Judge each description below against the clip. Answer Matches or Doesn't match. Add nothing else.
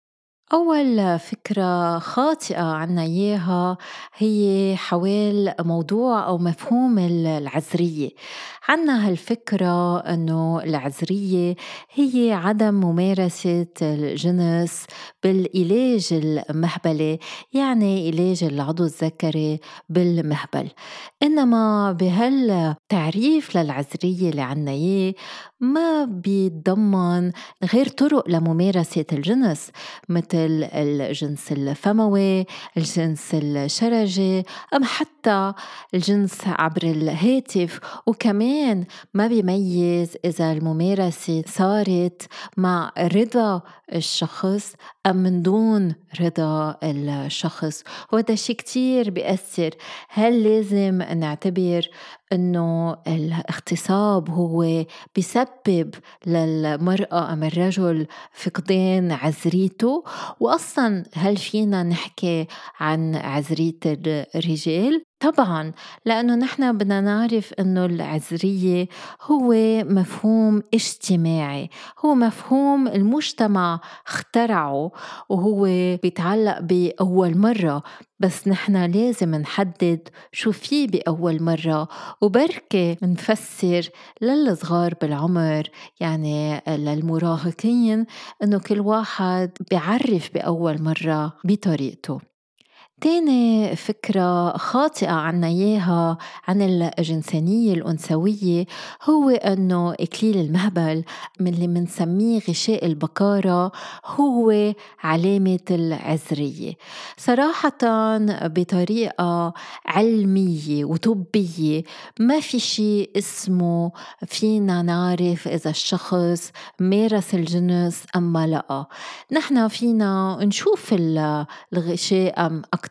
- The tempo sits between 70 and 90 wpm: Matches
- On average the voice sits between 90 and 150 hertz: Doesn't match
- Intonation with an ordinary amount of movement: Matches